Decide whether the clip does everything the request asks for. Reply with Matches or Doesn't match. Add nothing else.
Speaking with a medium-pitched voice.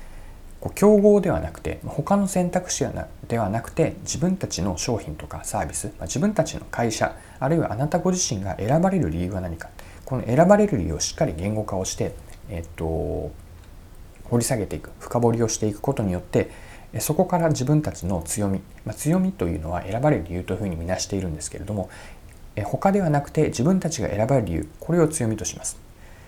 Doesn't match